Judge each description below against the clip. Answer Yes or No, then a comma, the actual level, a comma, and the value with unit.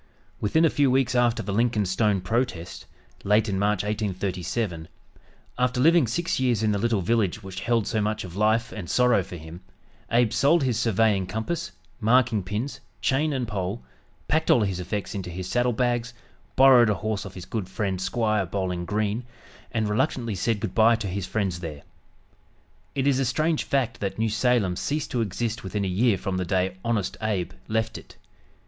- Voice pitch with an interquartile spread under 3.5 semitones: No, average, 4.0 semitones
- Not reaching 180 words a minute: No, average, 185 wpm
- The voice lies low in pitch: Yes, low, 110 Hz